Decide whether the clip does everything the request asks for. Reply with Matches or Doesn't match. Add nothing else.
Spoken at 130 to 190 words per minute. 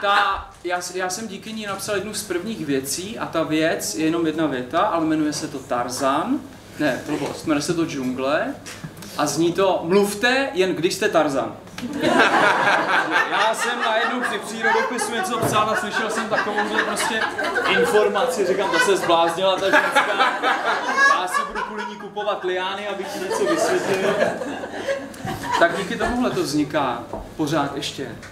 Matches